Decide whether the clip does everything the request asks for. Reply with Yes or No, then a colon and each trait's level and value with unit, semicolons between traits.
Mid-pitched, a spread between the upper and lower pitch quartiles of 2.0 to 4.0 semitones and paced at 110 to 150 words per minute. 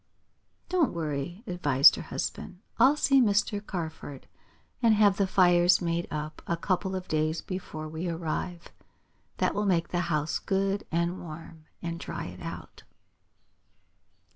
Yes: medium, 175 Hz; average, 3.5 semitones; average, 140 wpm